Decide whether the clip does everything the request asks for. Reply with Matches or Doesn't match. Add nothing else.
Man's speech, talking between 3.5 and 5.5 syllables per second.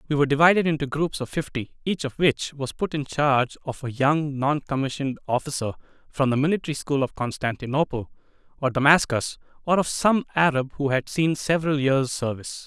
Doesn't match